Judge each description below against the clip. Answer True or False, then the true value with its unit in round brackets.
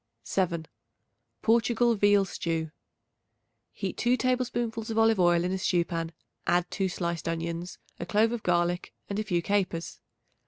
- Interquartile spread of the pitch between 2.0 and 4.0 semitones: False (4.5 semitones)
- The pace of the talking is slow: False (150 wpm)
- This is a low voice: False (190 Hz)